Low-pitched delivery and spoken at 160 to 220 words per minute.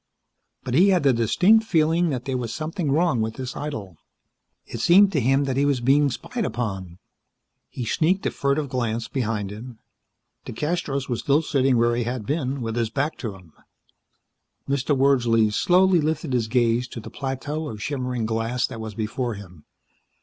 Yes: low, 130 Hz; average, 180 wpm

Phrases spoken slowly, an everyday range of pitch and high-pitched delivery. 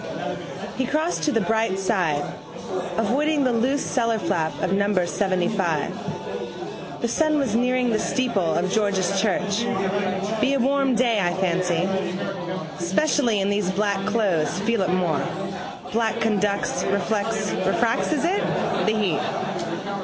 Yes: slow, 130 wpm; average, 4.1 semitones; high, 205 Hz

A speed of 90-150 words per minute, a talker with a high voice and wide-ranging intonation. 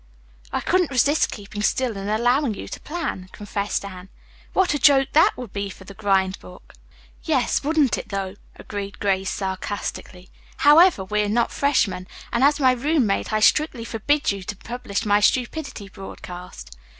No: average, 165 wpm; high, 215 Hz; wide, 5.9 semitones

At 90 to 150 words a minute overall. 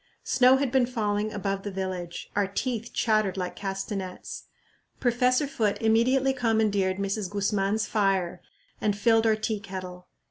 Yes: average, 140 wpm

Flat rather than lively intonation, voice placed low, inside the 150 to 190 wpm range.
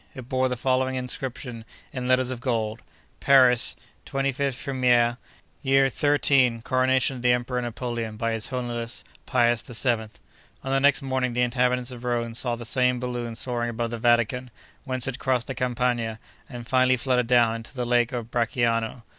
Yes: narrow, 1.6 semitones; low, 125 Hz; average, 170 wpm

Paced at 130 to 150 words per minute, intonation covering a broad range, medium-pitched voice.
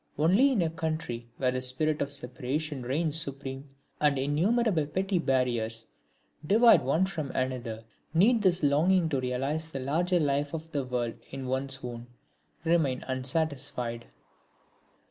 No: average, 140 wpm; average, 4.1 semitones; medium, 145 Hz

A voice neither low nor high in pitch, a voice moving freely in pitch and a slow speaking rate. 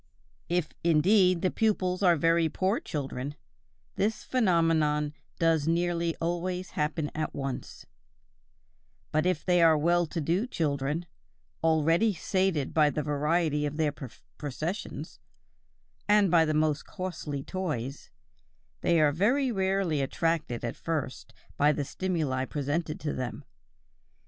No: medium, 165 Hz; average, 3.3 semitones; slow, 125 wpm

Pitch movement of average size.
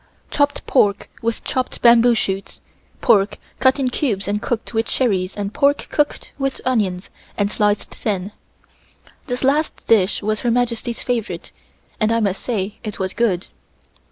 Yes: average, 3.5 semitones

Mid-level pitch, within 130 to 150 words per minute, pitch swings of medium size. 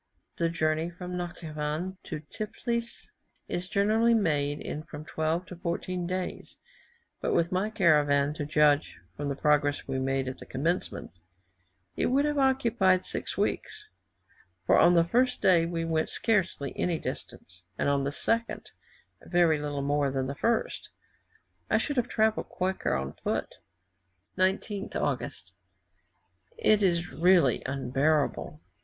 Yes: medium, 170 Hz; average, 140 wpm; average, 4.7 semitones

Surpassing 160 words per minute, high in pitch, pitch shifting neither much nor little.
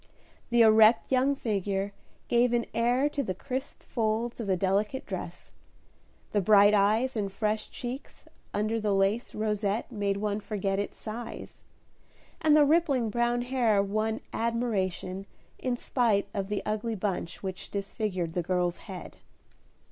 No: average, 145 wpm; high, 215 Hz; average, 3.2 semitones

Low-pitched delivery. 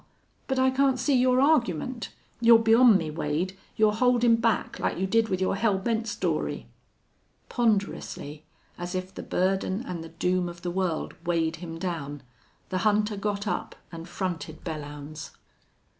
No: high, 190 Hz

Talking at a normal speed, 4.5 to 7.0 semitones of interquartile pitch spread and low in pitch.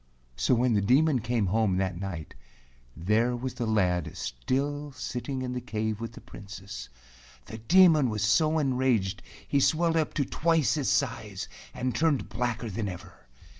Yes: average, 165 wpm; average, 5.2 semitones; low, 120 Hz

